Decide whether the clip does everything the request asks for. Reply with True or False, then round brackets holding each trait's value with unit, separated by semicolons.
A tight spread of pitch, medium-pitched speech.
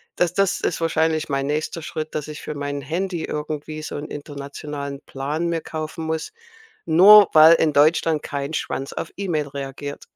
True (2.3 semitones; 155 Hz)